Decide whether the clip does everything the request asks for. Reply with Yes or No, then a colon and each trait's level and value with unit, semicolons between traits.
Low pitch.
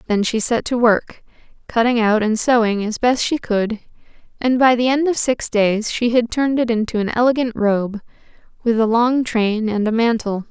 No: high, 230 Hz